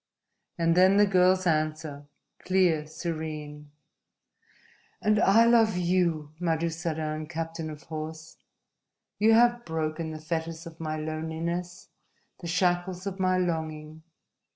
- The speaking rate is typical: No, slow, 115 wpm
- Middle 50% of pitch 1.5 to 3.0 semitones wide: Yes, average, 2.7 semitones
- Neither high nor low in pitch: Yes, medium, 165 Hz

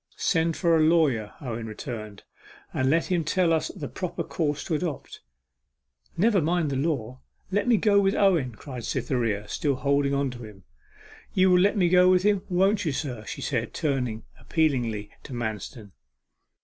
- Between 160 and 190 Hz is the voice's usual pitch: No, medium, 145 Hz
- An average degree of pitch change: No, wide, 6.8 semitones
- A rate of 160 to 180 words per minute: Yes, average, 175 wpm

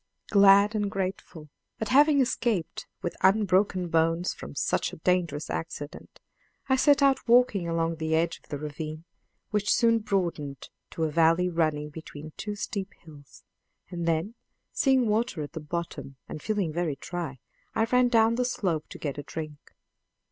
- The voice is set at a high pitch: No, medium, 175 Hz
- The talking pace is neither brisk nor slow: Yes, average, 160 wpm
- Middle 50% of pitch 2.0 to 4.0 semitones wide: No, average, 5.2 semitones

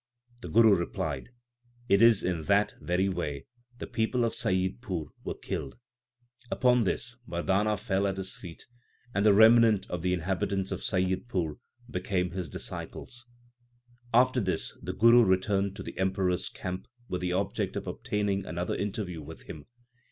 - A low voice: Yes, very low, 95 Hz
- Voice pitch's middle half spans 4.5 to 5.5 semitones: No, average, 3.5 semitones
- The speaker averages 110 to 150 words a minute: No, average, 160 wpm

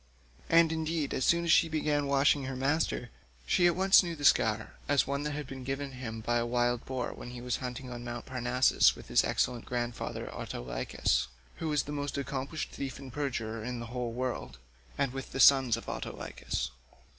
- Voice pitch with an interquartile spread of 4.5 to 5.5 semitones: No, average, 3.3 semitones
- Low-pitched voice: Yes, low, 130 Hz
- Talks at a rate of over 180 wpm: Yes, average, 190 wpm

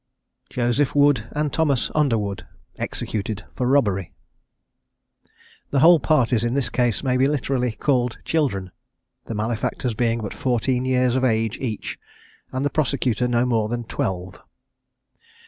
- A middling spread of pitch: Yes, average, 3.4 semitones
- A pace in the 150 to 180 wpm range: No, slow, 135 wpm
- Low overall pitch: Yes, low, 125 Hz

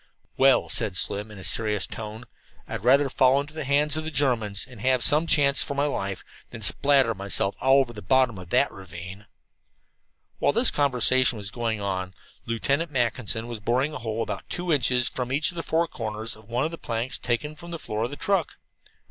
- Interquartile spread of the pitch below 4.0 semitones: No, average, 4.8 semitones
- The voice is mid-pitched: No, low, 125 Hz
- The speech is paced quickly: Yes, fast, 210 wpm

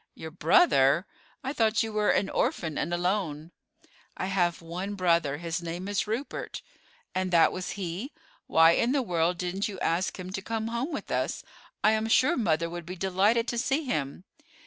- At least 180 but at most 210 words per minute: Yes, average, 185 wpm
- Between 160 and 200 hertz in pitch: Yes, medium, 185 Hz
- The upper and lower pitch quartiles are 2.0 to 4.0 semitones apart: No, average, 4.6 semitones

